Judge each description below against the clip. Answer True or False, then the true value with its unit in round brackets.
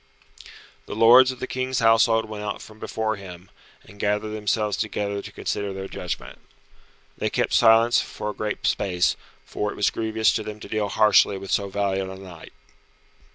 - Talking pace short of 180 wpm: False (185 wpm)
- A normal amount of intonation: False (2.0 semitones)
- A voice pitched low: True (105 Hz)